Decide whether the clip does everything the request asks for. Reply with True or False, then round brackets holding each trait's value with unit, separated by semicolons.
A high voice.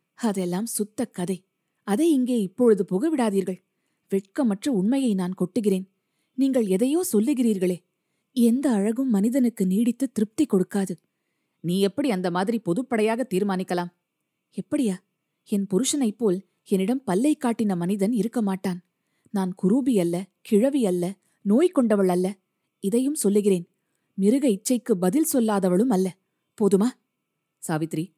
True (200 Hz)